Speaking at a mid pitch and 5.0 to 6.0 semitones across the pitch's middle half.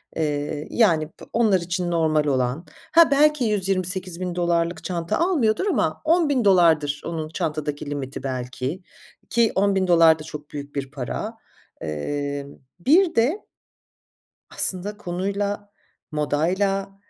Yes: medium, 175 Hz; average, 5.3 semitones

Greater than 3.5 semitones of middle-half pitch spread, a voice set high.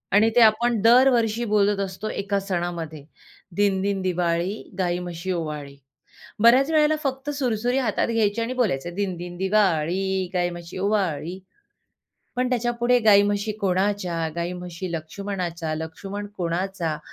Yes: average, 4.0 semitones; high, 195 Hz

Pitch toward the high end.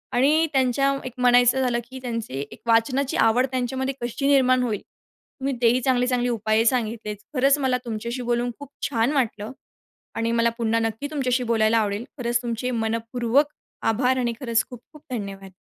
Yes: high, 245 Hz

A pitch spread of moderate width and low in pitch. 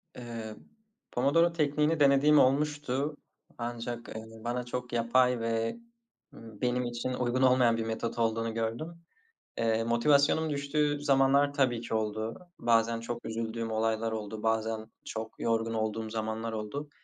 Yes: average, 3.4 semitones; low, 120 Hz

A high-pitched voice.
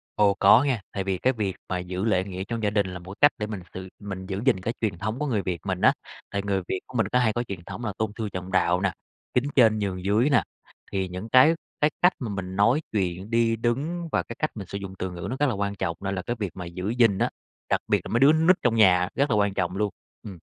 No: low, 100 Hz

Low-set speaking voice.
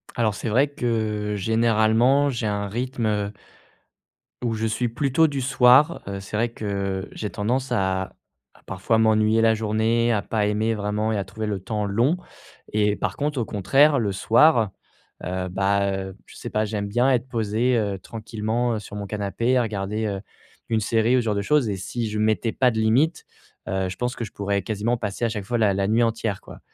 Yes: low, 110 Hz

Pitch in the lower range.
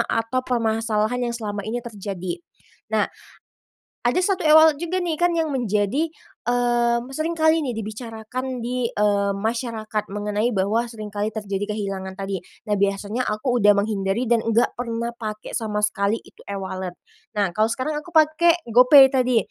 No: high, 225 Hz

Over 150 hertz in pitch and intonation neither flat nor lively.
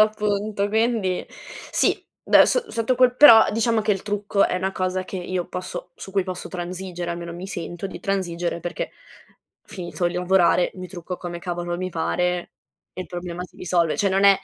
No: medium, 185 Hz; narrow, 2.3 semitones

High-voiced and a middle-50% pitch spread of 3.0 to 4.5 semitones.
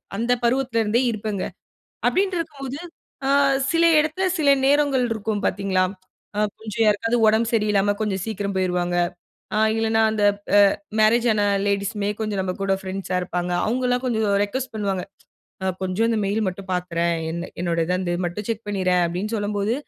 Yes: high, 210 Hz; average, 3.5 semitones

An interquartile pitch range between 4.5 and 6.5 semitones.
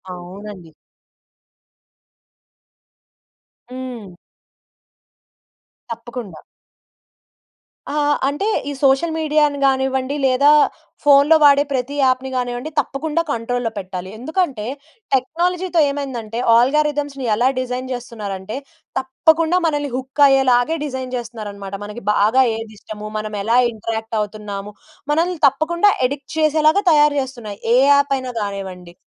Yes: average, 5.0 semitones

